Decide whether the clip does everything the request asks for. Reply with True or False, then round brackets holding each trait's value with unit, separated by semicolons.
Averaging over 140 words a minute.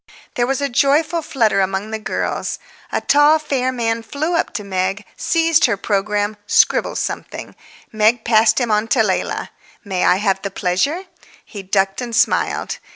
True (165 wpm)